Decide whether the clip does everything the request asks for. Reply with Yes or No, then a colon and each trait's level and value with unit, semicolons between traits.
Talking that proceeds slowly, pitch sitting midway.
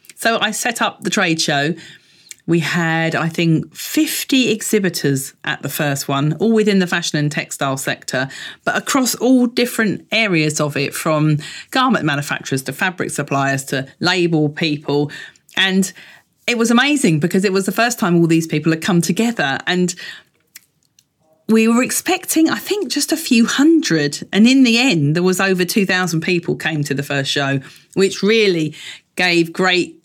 No: average, 170 wpm; medium, 175 Hz